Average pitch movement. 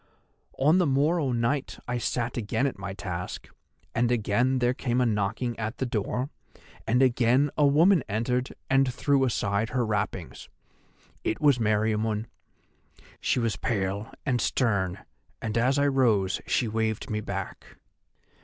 Yes: average, 3.7 semitones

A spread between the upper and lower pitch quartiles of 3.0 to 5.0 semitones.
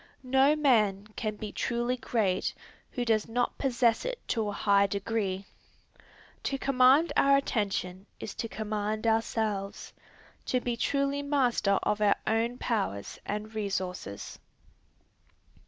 Yes: average, 3.7 semitones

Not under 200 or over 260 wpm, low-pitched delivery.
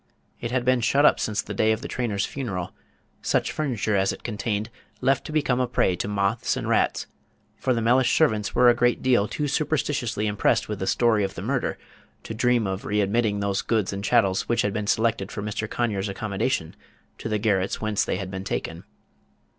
Yes: fast, 205 wpm; low, 110 Hz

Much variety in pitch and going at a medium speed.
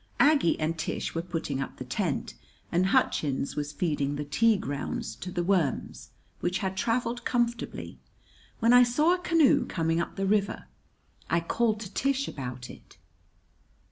Yes: wide, 7.6 semitones; average, 160 wpm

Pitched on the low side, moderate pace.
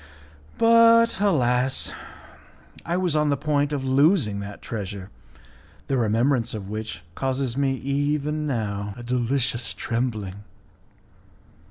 No: low, 130 Hz; slow, 115 wpm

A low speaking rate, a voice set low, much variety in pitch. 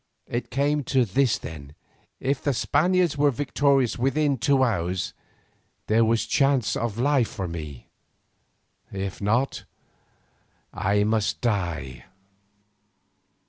Yes: slow, 115 wpm; low, 120 Hz; wide, 6.1 semitones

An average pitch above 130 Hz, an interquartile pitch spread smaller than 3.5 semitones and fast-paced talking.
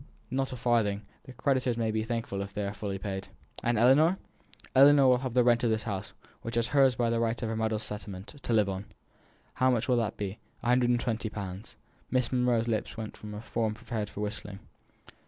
No: low, 115 Hz; average, 2.8 semitones; fast, 215 wpm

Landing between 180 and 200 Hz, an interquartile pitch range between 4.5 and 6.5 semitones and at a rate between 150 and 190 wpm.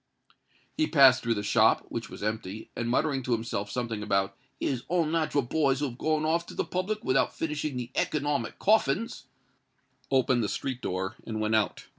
No: low, 130 Hz; wide, 5.6 semitones; average, 180 wpm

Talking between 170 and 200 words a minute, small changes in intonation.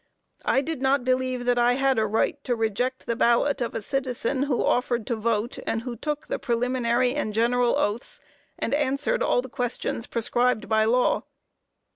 Yes: average, 175 wpm; narrow, 2.2 semitones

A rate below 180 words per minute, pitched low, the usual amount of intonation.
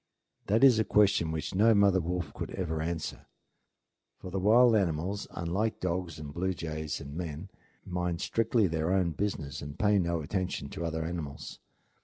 Yes: average, 170 wpm; very low, 90 Hz; average, 3.8 semitones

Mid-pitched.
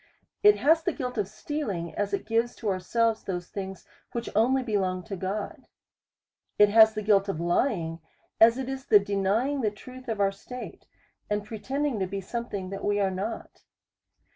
No: high, 210 Hz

